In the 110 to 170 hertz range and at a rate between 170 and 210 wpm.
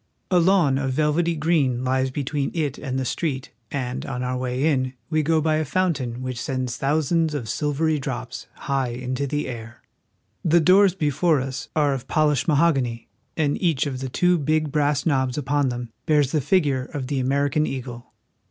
Yes: medium, 140 Hz; average, 185 wpm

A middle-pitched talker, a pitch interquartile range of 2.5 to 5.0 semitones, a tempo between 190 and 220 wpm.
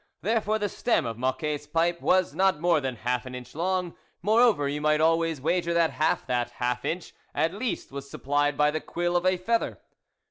Yes: medium, 160 Hz; average, 4.5 semitones; fast, 205 wpm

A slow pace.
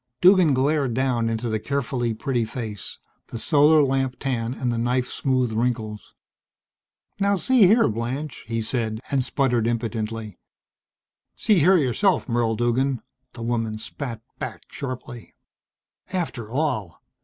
Yes: slow, 130 wpm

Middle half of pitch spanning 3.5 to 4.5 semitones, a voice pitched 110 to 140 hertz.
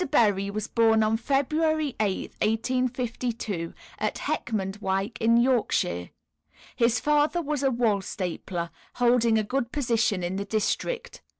No: average, 4.2 semitones; high, 230 Hz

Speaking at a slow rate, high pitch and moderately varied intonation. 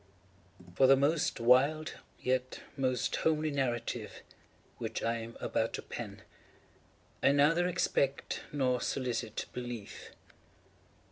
No: slow, 110 wpm; low, 130 Hz; average, 3.1 semitones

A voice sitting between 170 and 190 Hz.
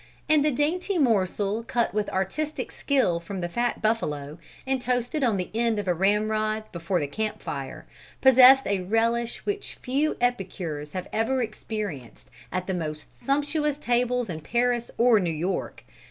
No: high, 225 Hz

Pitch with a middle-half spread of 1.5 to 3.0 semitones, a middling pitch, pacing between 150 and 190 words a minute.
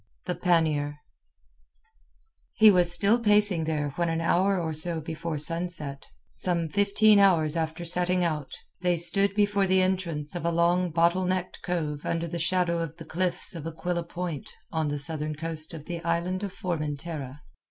Yes: narrow, 2.4 semitones; medium, 170 Hz; average, 160 wpm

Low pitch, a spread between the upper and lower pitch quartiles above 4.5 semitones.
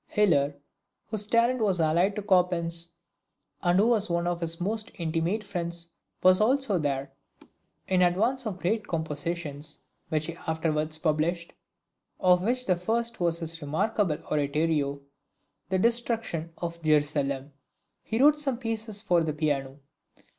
No: medium, 175 Hz; average, 5.1 semitones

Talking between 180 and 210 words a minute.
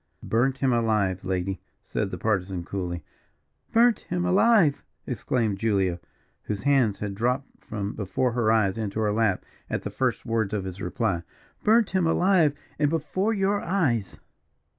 No: average, 155 wpm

